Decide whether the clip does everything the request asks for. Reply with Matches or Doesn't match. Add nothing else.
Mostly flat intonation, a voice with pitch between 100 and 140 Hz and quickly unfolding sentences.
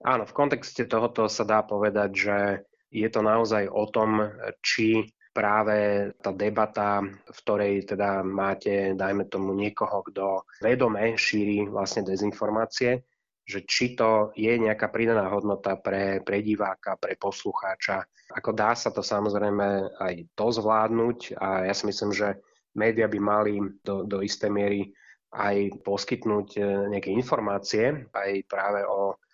Doesn't match